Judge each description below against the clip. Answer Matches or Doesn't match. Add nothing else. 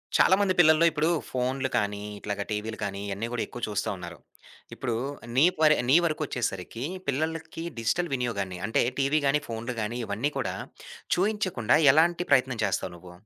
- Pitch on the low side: Matches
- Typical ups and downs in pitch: Doesn't match